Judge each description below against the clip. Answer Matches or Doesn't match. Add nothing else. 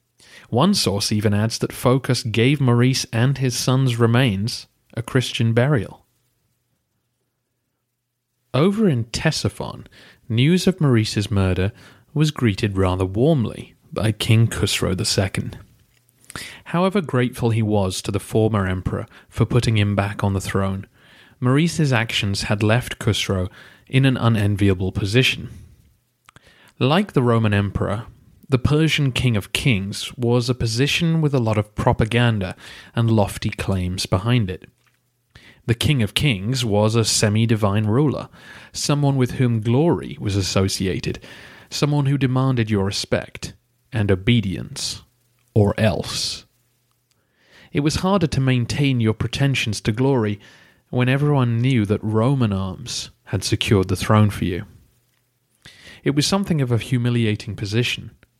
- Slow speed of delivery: Matches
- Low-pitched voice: Matches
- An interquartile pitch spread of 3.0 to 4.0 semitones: Matches